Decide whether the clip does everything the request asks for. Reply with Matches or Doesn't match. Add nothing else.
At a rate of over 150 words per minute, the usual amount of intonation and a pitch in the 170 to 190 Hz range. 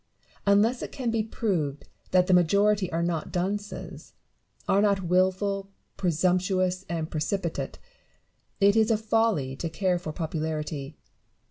Doesn't match